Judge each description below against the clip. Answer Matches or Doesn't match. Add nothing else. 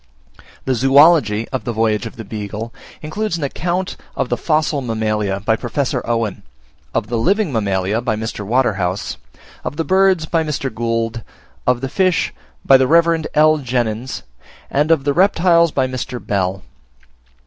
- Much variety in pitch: Matches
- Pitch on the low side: Matches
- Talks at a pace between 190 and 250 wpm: Doesn't match